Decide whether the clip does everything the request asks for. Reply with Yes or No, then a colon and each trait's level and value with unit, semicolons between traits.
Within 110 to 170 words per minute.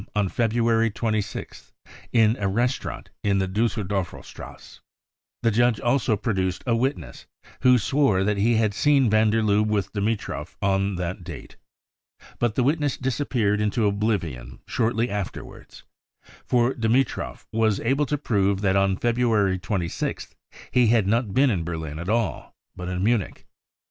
Yes: average, 145 wpm